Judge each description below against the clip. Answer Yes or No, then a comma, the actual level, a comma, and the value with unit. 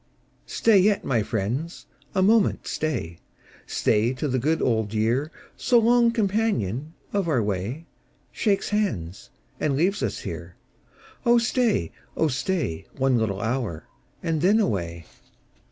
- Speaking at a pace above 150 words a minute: No, slow, 135 wpm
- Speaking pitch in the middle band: Yes, medium, 145 Hz